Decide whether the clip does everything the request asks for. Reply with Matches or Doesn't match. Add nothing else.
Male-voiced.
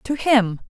Doesn't match